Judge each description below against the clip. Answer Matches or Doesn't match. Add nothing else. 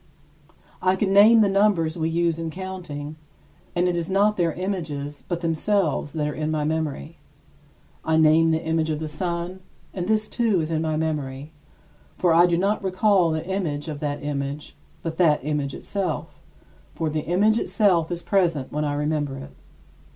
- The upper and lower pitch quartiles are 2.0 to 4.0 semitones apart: Matches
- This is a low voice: Doesn't match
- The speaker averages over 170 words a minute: Matches